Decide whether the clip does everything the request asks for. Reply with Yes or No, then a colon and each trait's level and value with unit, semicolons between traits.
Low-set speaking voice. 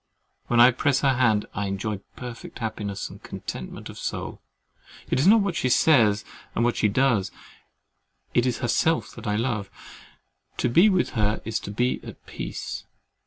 Yes: low, 120 Hz